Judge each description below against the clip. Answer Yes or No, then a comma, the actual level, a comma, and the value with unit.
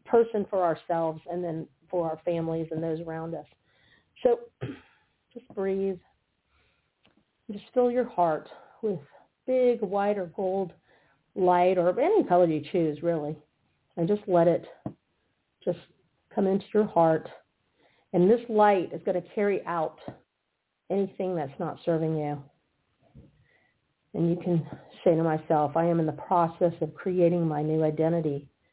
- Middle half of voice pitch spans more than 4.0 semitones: No, average, 3.3 semitones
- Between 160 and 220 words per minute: No, average, 145 wpm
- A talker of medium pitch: Yes, medium, 175 Hz